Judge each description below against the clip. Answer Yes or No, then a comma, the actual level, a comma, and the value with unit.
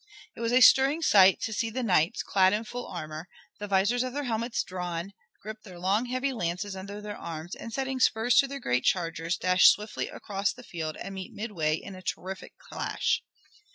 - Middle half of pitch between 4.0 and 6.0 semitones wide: Yes, average, 4.6 semitones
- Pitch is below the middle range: No, high, 200 Hz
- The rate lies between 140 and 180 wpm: No, average, 200 wpm